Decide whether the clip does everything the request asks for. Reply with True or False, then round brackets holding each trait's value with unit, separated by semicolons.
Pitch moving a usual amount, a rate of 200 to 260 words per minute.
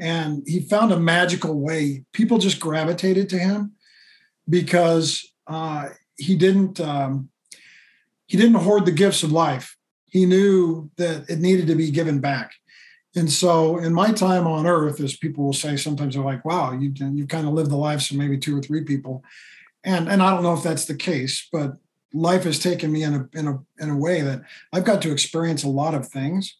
True (3.8 semitones; 205 wpm)